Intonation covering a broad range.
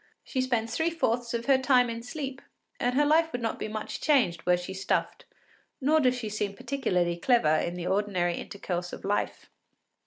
Yes: wide, 5.7 semitones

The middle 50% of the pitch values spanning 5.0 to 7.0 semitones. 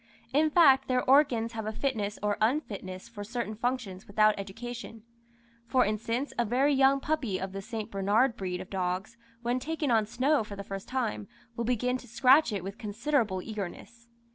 No: average, 4.1 semitones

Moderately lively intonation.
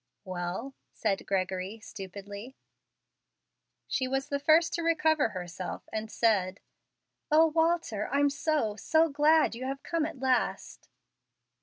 No: wide, 7.5 semitones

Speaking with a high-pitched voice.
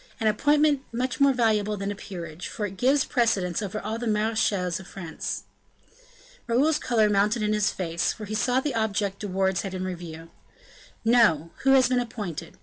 Yes: high, 210 Hz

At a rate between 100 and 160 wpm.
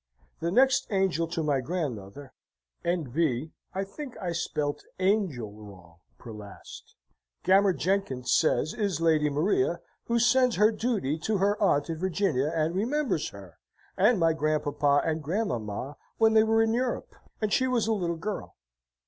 Yes: average, 155 wpm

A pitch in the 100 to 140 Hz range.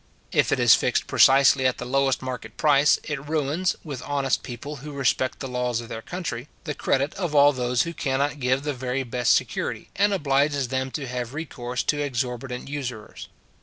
Yes: low, 135 Hz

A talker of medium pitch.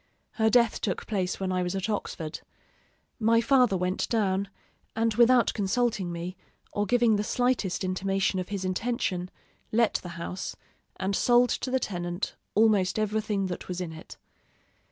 No: high, 200 Hz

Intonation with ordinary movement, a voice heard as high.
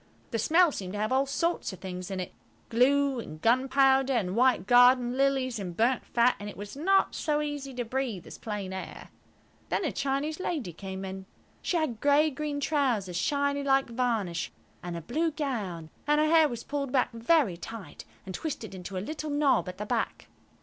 No: wide, 6.2 semitones; very high, 250 Hz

